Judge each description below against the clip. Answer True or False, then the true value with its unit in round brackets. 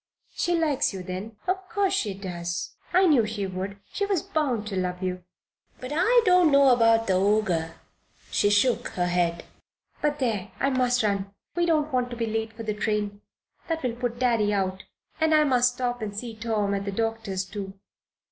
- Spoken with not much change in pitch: False (5.5 semitones)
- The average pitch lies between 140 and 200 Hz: False (225 Hz)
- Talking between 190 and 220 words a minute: True (195 wpm)